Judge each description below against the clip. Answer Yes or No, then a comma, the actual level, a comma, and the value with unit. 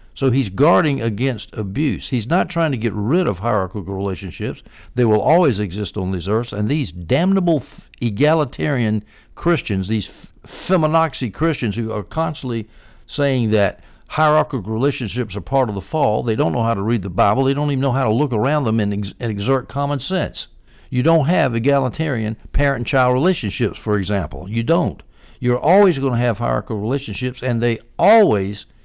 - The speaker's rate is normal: Yes, average, 180 wpm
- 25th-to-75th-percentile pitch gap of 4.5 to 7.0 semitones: Yes, average, 5.0 semitones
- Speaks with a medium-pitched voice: No, low, 120 Hz